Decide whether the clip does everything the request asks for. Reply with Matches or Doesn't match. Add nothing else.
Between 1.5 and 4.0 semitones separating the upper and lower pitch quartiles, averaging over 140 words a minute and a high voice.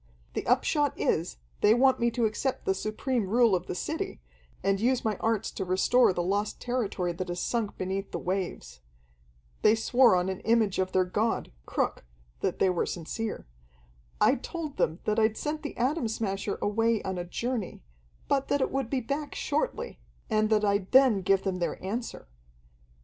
Doesn't match